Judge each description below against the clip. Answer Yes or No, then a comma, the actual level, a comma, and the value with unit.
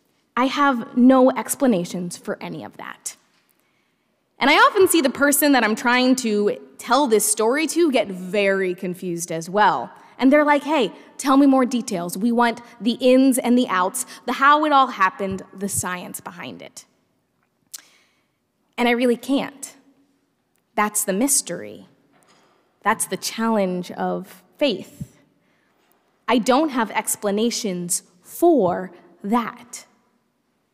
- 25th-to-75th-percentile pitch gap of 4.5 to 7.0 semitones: Yes, average, 5.3 semitones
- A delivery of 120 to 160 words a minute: Yes, slow, 135 wpm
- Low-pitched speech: No, high, 235 Hz